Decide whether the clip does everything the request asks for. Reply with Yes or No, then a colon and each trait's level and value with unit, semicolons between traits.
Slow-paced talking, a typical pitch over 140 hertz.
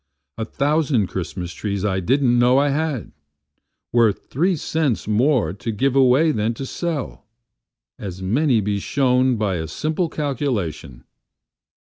No: slow, 120 wpm; low, 120 Hz